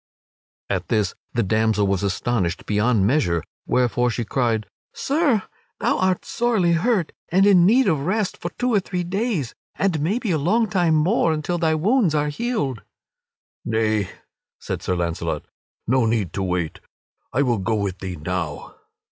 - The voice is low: No, medium, 145 Hz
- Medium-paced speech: Yes, average, 160 wpm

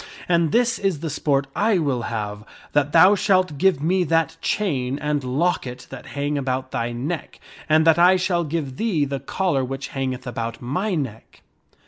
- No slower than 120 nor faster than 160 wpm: No, average, 175 wpm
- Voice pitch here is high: No, medium, 150 Hz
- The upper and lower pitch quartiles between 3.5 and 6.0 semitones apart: Yes, average, 5.2 semitones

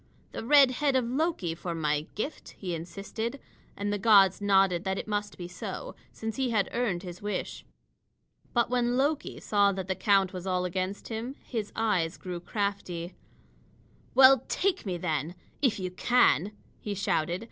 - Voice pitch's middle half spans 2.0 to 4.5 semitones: No, average, 4.9 semitones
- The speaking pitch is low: No, high, 200 Hz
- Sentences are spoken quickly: No, average, 170 wpm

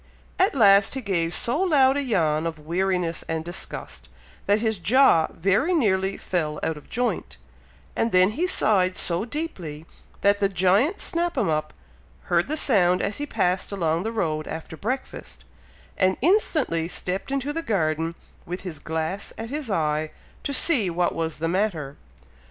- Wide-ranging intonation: Yes, wide, 6.9 semitones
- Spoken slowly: No, average, 165 wpm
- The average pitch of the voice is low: No, high, 190 Hz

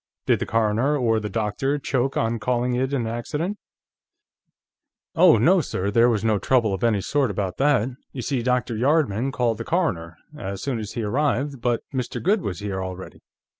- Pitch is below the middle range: Yes, low, 120 Hz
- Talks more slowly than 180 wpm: No, average, 185 wpm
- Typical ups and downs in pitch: Yes, average, 4.5 semitones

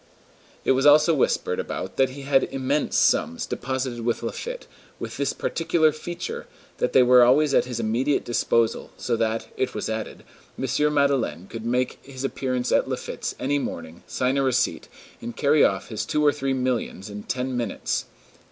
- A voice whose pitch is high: No, low, 130 Hz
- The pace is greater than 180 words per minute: No, average, 175 wpm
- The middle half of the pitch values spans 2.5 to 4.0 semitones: Yes, average, 3.2 semitones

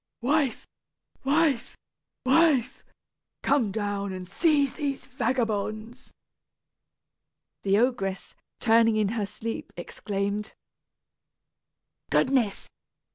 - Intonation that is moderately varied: Yes, average, 4.8 semitones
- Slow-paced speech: Yes, slow, 80 wpm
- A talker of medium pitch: No, high, 230 Hz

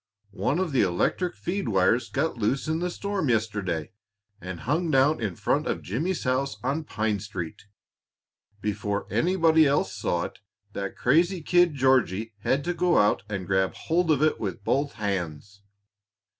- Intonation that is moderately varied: No, wide, 7.9 semitones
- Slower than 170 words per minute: Yes, average, 160 wpm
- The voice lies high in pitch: No, low, 130 Hz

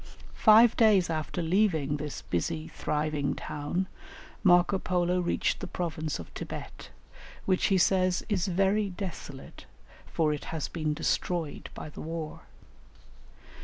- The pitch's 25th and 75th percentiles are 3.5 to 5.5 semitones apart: Yes, average, 3.8 semitones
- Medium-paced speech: No, slow, 130 wpm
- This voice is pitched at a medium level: Yes, medium, 175 Hz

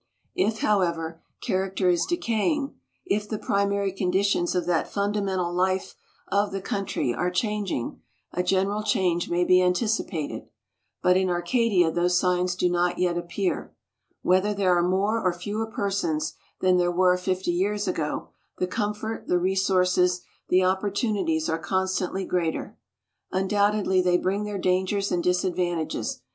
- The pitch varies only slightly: Yes, narrow, 2.1 semitones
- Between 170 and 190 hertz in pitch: Yes, medium, 185 Hz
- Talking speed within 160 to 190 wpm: No, average, 140 wpm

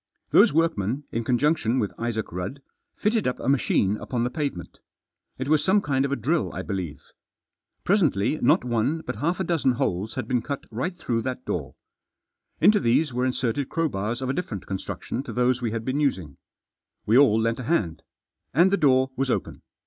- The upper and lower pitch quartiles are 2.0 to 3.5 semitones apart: No, average, 4.8 semitones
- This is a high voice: No, low, 130 Hz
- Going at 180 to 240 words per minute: Yes, average, 195 wpm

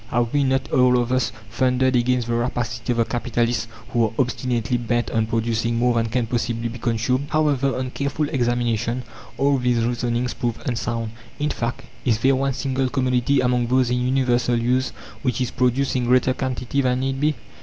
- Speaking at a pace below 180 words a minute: No, average, 185 wpm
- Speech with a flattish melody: Yes, narrow, 1.7 semitones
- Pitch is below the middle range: Yes, low, 125 Hz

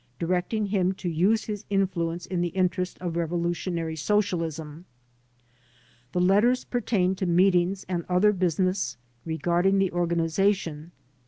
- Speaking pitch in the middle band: Yes, medium, 180 Hz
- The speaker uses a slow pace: Yes, slow, 130 wpm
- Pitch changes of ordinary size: No, narrow, 2.3 semitones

